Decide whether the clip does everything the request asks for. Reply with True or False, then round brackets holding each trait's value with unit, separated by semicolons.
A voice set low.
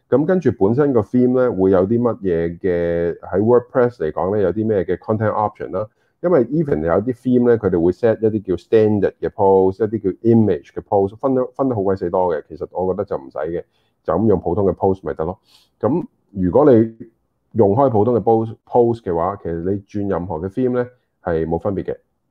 True (110 Hz)